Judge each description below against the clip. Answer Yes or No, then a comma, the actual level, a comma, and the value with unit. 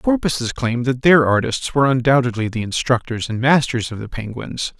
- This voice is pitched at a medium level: No, low, 125 Hz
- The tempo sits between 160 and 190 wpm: No, average, 200 wpm